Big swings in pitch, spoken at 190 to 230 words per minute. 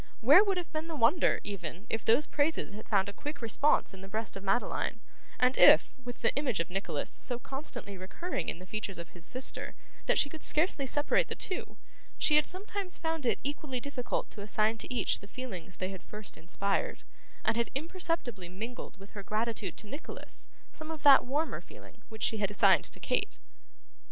Yes: wide, 6.7 semitones; average, 200 wpm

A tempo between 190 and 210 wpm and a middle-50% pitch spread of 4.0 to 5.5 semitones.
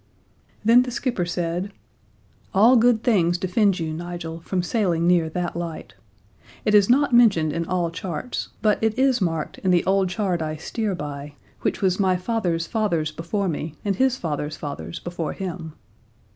No: average, 170 wpm; average, 4.3 semitones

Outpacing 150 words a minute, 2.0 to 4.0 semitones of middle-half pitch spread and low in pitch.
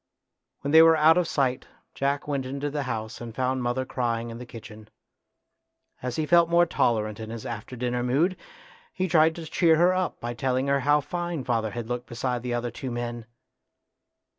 No: average, 195 wpm; average, 4.5 semitones; low, 130 Hz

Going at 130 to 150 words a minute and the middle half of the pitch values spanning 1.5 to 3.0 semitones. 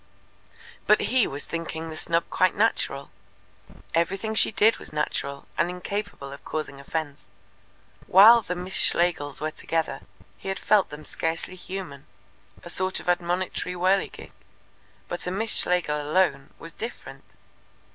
No: average, 140 wpm; average, 3.8 semitones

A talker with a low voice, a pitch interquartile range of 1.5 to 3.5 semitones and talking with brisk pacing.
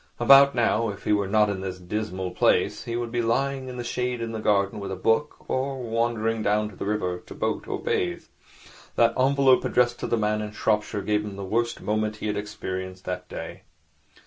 Yes: low, 110 Hz; average, 2.9 semitones; fast, 215 wpm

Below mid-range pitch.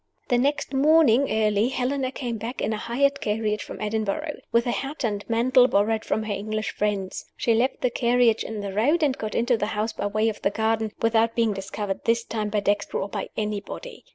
No: high, 225 Hz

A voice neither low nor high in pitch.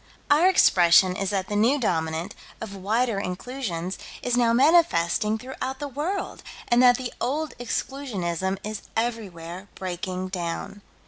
No: high, 215 Hz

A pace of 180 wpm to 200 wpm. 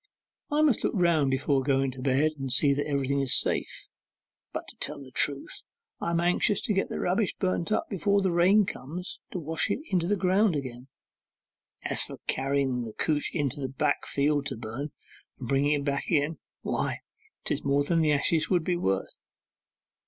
Yes: average, 185 wpm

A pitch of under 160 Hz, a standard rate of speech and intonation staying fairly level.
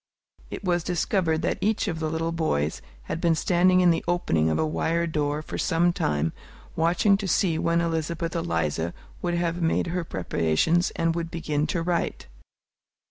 No: medium, 165 Hz; average, 175 wpm; narrow, 1.9 semitones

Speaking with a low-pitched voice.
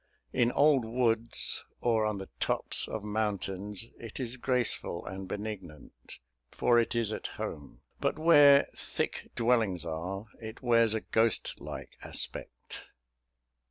Yes: low, 110 Hz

